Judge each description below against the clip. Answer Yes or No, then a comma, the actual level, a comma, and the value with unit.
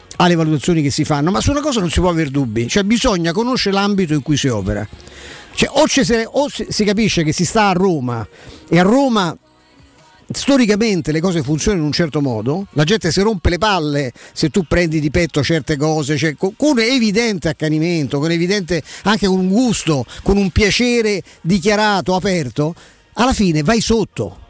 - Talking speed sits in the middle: No, fast, 185 wpm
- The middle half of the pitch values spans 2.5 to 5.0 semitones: No, wide, 5.5 semitones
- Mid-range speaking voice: Yes, medium, 175 Hz